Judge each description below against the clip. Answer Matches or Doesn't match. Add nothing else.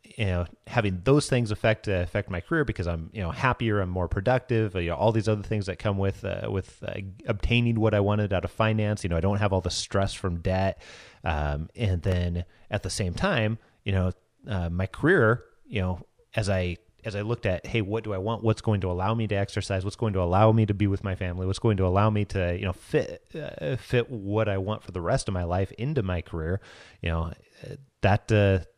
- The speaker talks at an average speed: Doesn't match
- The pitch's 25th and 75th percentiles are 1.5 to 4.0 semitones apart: Matches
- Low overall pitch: Matches